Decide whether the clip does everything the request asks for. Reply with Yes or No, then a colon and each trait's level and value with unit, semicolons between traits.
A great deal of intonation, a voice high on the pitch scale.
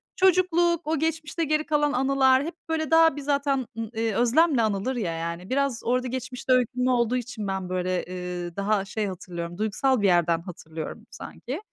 Yes: wide, 6.9 semitones; high, 245 Hz